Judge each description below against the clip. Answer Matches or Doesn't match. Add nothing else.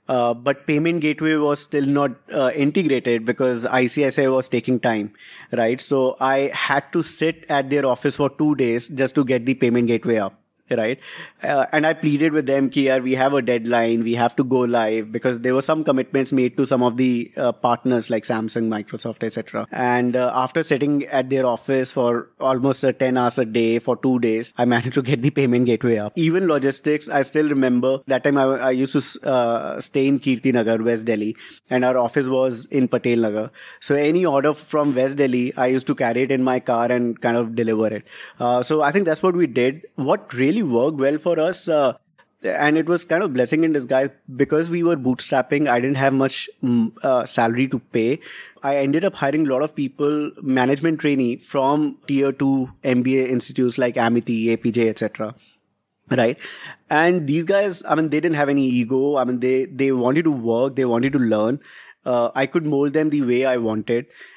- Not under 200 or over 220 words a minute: Matches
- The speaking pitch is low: Matches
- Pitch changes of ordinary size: Matches